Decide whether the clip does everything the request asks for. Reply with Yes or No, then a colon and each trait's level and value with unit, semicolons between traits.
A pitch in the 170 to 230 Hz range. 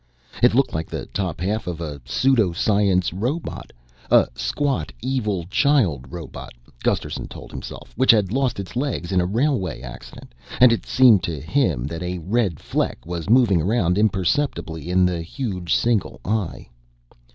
No: very low, 95 Hz